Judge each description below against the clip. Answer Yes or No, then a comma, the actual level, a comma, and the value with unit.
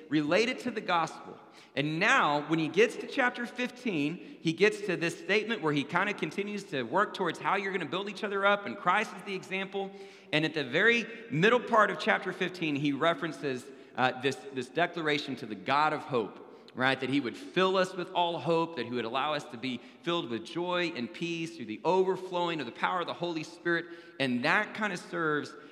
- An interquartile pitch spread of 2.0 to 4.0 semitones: No, average, 4.9 semitones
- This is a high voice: No, medium, 170 Hz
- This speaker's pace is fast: Yes, fast, 220 wpm